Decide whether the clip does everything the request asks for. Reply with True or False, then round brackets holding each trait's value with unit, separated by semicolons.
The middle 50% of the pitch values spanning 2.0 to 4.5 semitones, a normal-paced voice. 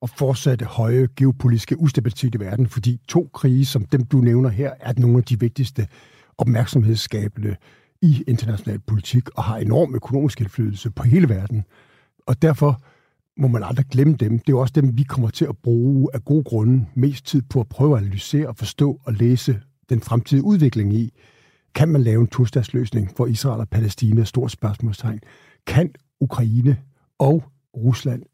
True (3.4 semitones; 175 wpm)